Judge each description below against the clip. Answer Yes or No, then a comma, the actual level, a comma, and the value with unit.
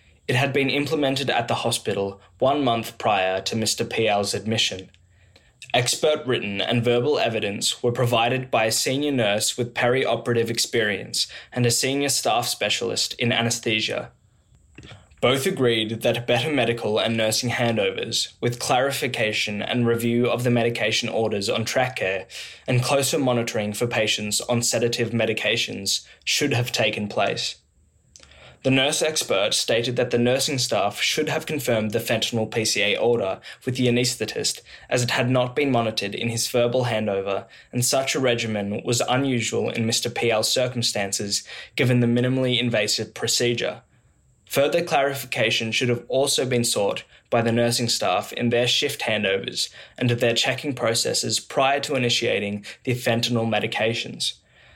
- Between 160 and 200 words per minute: No, average, 145 wpm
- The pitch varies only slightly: Yes, narrow, 2.3 semitones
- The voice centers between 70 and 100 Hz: No, low, 120 Hz